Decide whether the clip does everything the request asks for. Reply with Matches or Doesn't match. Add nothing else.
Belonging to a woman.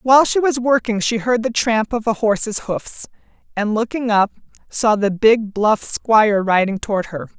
Matches